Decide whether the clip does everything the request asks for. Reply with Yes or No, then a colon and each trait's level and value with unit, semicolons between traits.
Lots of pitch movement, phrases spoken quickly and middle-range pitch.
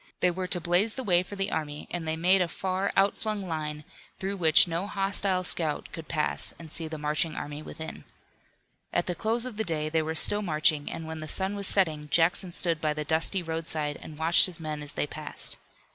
No: average, 3.5 semitones; fast, 220 wpm; medium, 165 Hz